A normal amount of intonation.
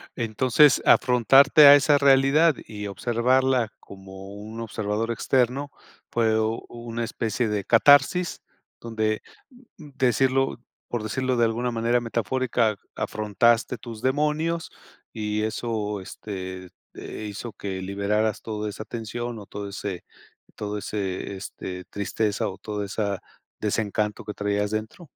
Yes: average, 3.3 semitones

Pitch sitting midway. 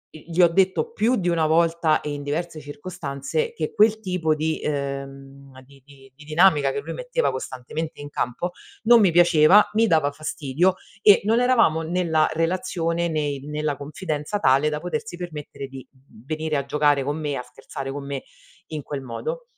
Yes: medium, 155 Hz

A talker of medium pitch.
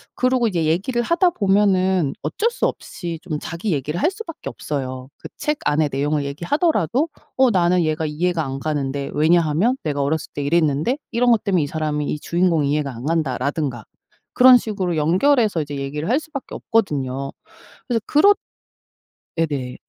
Yes: medium, 165 Hz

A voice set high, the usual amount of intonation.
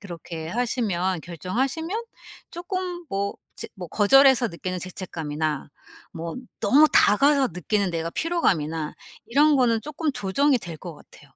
No: high, 205 Hz; wide, 8.7 semitones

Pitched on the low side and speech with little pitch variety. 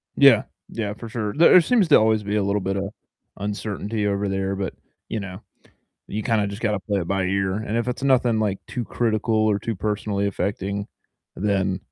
Yes: low, 105 Hz; narrow, 2.1 semitones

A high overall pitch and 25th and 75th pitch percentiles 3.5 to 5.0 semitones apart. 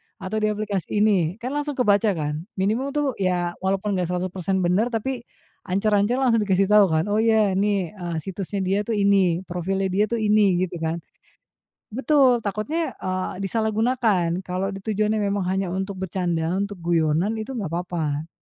No: high, 195 Hz; average, 3.1 semitones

